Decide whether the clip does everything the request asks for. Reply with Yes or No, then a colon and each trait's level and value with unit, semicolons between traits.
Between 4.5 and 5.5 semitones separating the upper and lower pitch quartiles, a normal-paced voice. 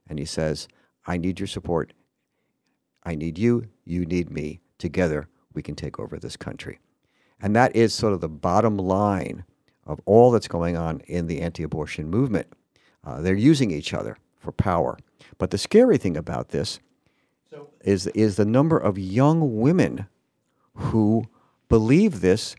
Yes: average, 5.2 semitones; average, 160 wpm